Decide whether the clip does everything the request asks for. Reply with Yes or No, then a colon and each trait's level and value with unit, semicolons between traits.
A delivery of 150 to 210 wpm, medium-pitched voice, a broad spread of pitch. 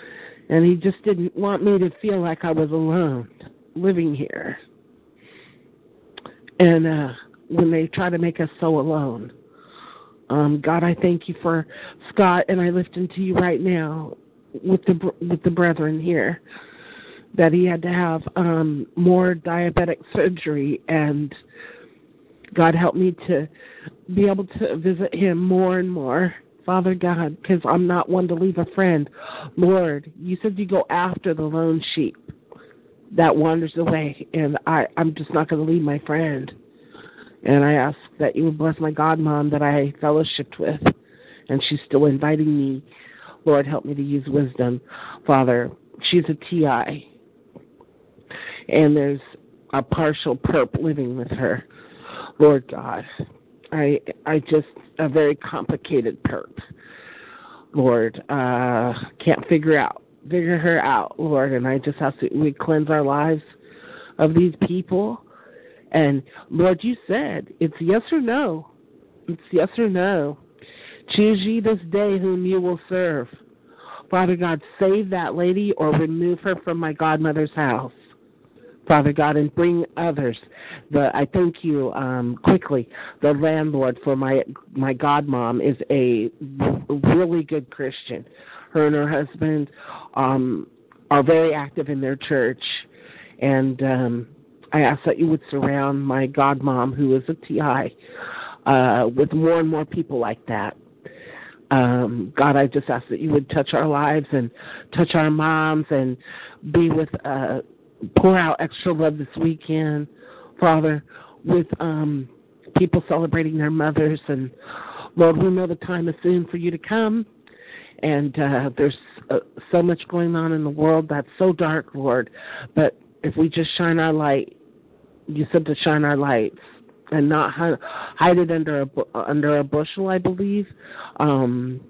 No: average, 155 wpm; medium, 155 Hz; average, 3.5 semitones